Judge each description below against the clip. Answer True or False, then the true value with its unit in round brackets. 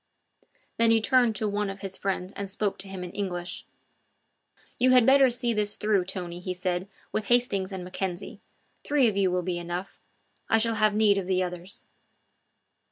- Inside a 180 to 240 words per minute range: True (185 wpm)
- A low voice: False (195 Hz)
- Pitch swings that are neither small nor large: True (3.2 semitones)